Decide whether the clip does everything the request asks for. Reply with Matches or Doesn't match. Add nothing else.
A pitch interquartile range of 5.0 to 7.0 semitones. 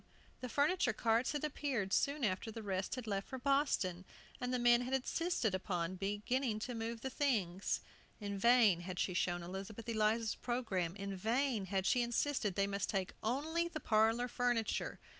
Doesn't match